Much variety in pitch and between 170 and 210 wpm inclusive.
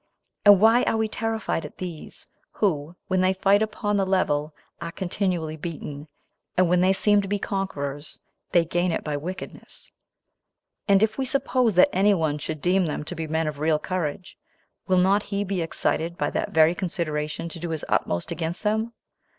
No: average, 4.1 semitones; average, 185 wpm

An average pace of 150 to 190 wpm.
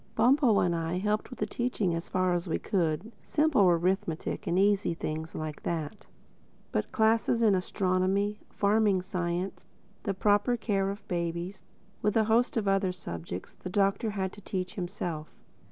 Yes: average, 160 wpm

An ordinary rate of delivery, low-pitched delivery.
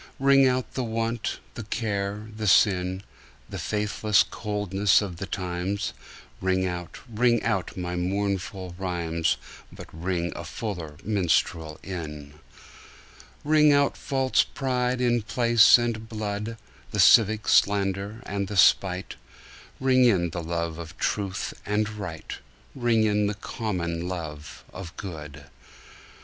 No: slow, 130 wpm; low, 100 Hz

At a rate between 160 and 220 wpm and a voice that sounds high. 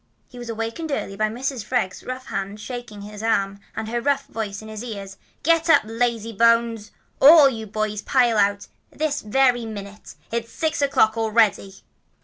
Yes: average, 180 wpm; high, 225 Hz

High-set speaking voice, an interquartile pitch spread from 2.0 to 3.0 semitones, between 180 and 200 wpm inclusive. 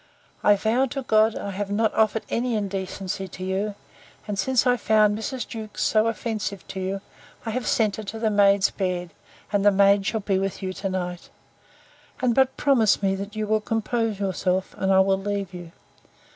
Yes: high, 205 Hz; narrow, 2.4 semitones; average, 195 wpm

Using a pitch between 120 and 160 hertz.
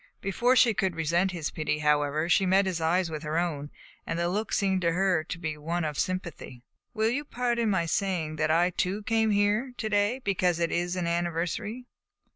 No: medium, 180 Hz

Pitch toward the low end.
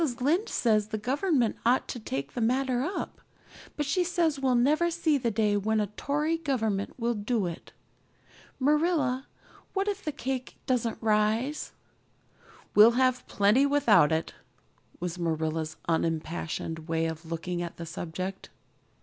No: high, 235 Hz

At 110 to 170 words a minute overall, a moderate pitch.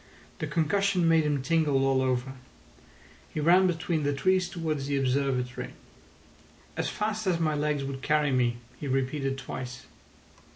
Yes: average, 150 wpm; medium, 145 Hz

